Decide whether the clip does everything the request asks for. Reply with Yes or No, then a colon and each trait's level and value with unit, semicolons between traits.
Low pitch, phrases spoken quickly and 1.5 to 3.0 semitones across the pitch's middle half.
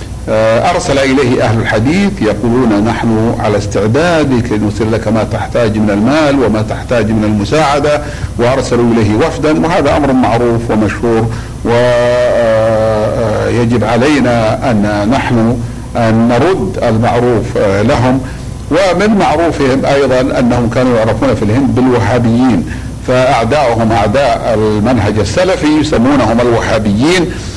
No: low, 115 Hz; average, 105 wpm; narrow, 2.6 semitones